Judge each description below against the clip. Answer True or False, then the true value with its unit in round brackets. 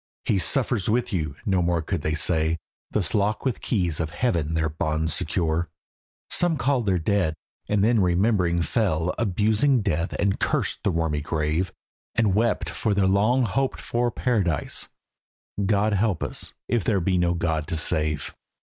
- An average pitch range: True (5.0 semitones)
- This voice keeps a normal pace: True (165 wpm)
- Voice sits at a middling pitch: False (95 Hz)